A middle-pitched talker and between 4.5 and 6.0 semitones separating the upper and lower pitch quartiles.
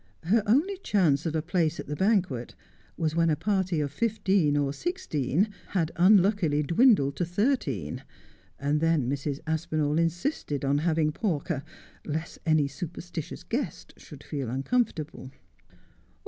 Yes: medium, 160 Hz; average, 4.9 semitones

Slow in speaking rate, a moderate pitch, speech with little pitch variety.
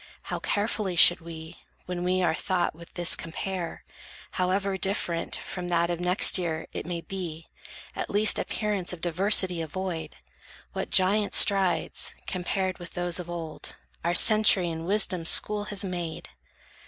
No: average, 150 wpm; medium, 180 Hz; narrow, 2.3 semitones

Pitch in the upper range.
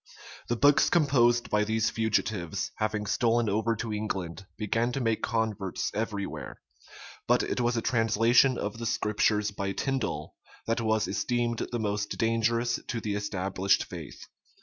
No: low, 110 Hz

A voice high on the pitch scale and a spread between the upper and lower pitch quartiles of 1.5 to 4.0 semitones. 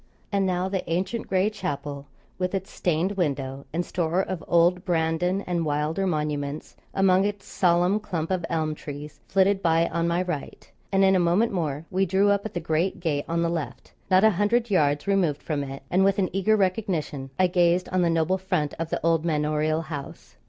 No: medium, 175 Hz; average, 3.4 semitones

